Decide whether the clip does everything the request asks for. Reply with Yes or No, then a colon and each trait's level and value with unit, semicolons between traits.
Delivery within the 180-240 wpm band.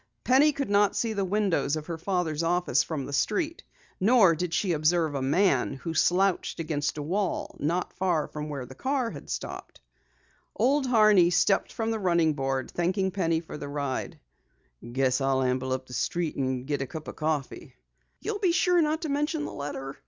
Yes: average, 190 wpm